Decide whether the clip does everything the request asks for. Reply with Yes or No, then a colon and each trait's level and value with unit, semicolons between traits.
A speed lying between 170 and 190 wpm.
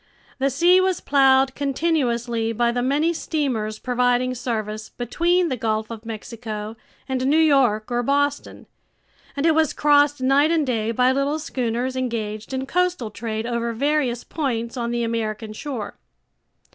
No: average, 150 wpm